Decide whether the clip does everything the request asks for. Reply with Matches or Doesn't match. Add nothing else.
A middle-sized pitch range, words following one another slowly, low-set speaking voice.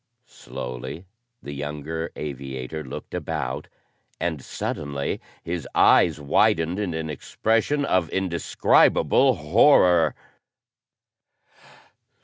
Matches